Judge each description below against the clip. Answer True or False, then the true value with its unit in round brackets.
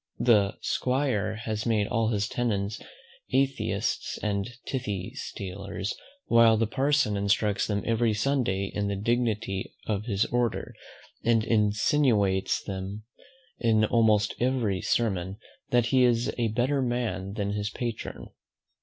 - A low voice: True (110 Hz)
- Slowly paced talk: True (130 wpm)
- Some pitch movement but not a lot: True (3.1 semitones)